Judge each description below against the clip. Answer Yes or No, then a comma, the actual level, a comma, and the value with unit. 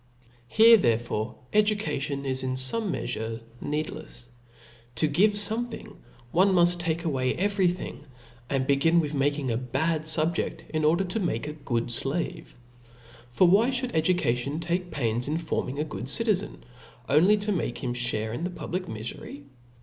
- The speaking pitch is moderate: Yes, medium, 155 Hz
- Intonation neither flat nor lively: No, wide, 5.9 semitones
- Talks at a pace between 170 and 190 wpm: No, average, 155 wpm